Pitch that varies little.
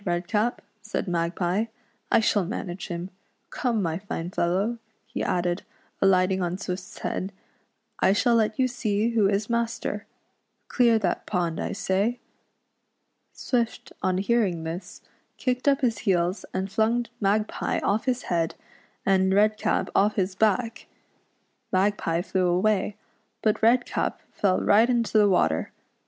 No: average, 3.6 semitones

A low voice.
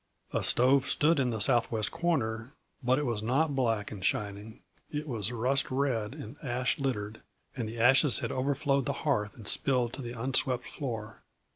Yes: low, 125 Hz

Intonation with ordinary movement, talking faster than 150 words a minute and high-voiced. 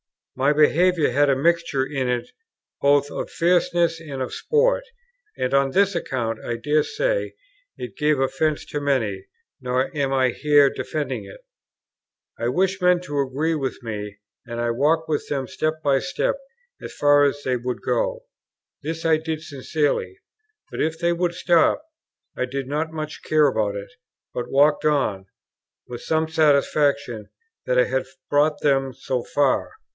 No: average, 3.7 semitones; average, 160 wpm; medium, 145 Hz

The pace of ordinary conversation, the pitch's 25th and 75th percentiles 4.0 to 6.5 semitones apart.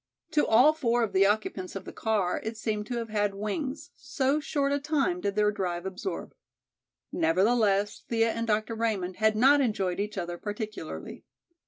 No: average, 175 wpm; average, 3.6 semitones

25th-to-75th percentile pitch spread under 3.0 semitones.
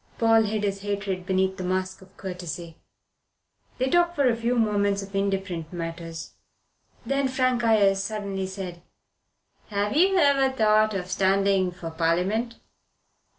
No: average, 3.3 semitones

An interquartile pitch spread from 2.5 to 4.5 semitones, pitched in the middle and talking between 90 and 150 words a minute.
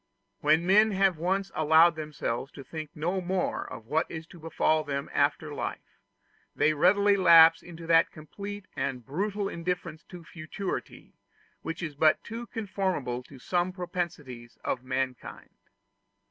Yes: average, 3.7 semitones; medium, 165 Hz; average, 145 wpm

